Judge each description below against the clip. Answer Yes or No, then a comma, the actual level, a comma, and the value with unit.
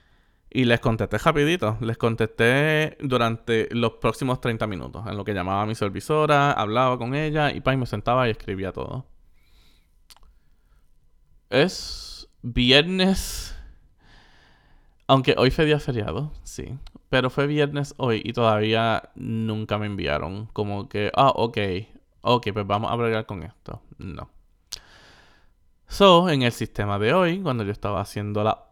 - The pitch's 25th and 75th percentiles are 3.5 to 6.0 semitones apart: Yes, average, 4.3 semitones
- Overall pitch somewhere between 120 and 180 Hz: No, low, 110 Hz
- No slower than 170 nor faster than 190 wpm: No, average, 140 wpm